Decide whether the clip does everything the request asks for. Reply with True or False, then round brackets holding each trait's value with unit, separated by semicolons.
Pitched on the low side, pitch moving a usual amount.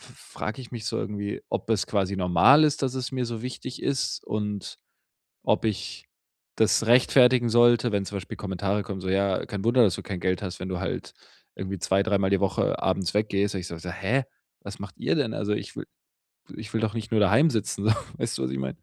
True (105 Hz; 3.5 semitones)